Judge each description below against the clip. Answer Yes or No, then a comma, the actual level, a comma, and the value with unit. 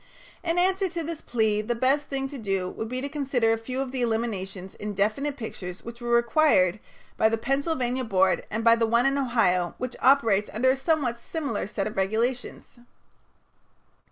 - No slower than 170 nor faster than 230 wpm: Yes, average, 185 wpm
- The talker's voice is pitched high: Yes, high, 235 Hz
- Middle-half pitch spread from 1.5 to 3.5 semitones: No, average, 4.2 semitones